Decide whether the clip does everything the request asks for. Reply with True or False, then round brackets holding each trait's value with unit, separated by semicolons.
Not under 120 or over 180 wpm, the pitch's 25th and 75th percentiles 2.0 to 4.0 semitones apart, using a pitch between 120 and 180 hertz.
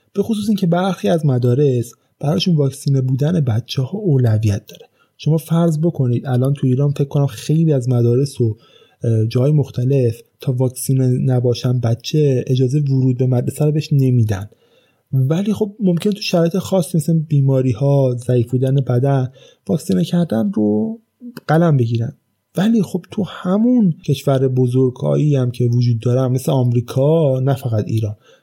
False (150 wpm; 4.7 semitones; 135 Hz)